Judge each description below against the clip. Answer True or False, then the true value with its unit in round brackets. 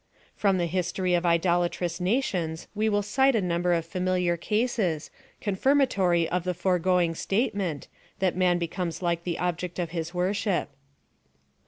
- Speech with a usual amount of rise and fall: False (2.1 semitones)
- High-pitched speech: False (180 Hz)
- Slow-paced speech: False (150 wpm)